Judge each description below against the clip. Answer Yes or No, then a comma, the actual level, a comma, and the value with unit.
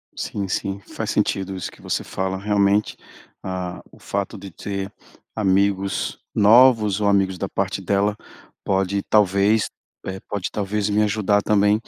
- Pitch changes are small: Yes, narrow, 1.4 semitones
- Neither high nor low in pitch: No, low, 100 Hz